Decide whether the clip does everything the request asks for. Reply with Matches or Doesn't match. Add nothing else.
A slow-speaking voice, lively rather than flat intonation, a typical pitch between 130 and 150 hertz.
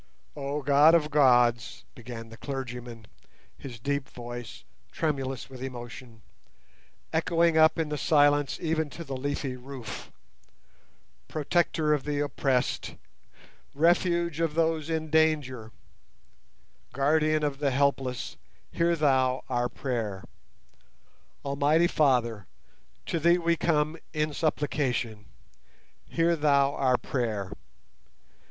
Doesn't match